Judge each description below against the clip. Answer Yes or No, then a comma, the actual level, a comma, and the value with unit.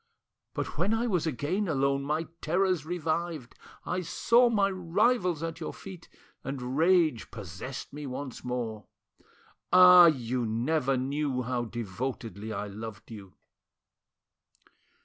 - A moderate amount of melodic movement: No, wide, 6.4 semitones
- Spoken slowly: Yes, slow, 125 wpm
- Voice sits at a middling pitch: Yes, medium, 145 Hz